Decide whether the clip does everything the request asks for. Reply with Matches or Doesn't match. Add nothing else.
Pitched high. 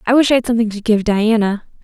Matches